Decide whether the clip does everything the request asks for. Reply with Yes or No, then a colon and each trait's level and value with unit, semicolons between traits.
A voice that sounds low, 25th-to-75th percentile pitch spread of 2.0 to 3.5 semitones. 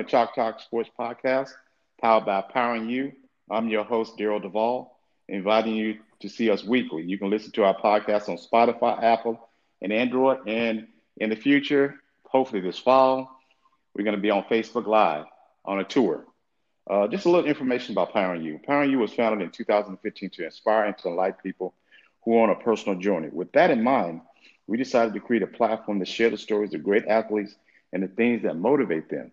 Yes: low, 115 Hz; average, 3.2 semitones